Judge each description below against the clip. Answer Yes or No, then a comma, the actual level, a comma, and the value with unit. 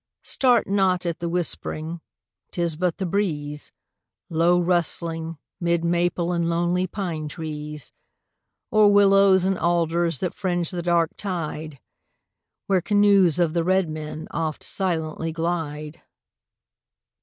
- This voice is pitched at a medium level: Yes, medium, 170 Hz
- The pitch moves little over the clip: Yes, narrow, 2.2 semitones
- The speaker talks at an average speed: No, slow, 120 wpm